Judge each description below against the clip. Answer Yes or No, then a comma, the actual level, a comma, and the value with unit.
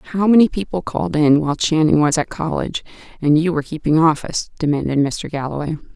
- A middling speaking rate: Yes, average, 180 wpm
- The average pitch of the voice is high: No, medium, 155 Hz